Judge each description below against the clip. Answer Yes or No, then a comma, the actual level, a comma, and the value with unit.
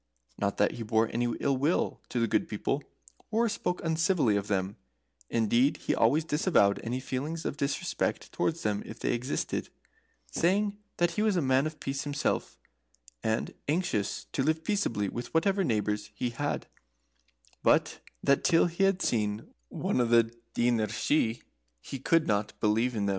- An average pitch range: No, wide, 6.7 semitones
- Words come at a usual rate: Yes, average, 170 wpm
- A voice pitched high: No, low, 130 Hz